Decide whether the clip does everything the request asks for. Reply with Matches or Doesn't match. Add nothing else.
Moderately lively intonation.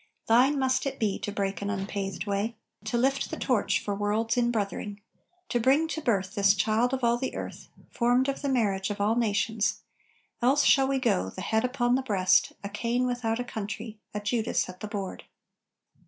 Matches